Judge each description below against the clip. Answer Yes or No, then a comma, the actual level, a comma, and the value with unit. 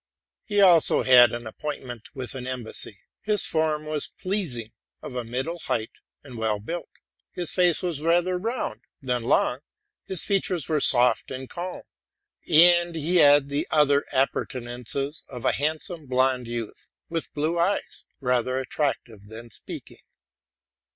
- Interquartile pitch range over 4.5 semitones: Yes, average, 5.3 semitones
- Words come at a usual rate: Yes, average, 145 wpm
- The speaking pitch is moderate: Yes, medium, 145 Hz